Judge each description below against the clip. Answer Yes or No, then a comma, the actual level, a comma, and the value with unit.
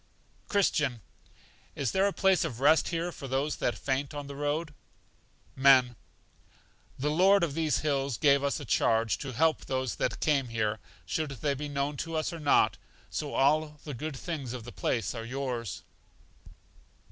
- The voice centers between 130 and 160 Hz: Yes, medium, 140 Hz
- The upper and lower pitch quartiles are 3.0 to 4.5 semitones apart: Yes, average, 3.3 semitones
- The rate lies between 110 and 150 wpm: No, average, 170 wpm